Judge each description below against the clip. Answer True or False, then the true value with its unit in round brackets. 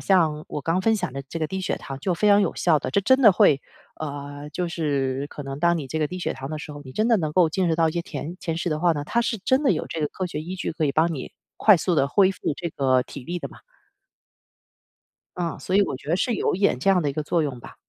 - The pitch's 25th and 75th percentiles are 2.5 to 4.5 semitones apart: True (4.2 semitones)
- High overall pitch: False (165 Hz)